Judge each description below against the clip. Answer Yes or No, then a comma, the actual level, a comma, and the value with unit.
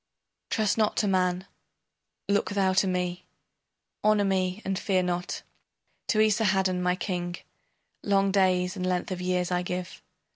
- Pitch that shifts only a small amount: Yes, narrow, 1.6 semitones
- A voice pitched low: No, medium, 185 Hz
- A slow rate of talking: No, average, 145 wpm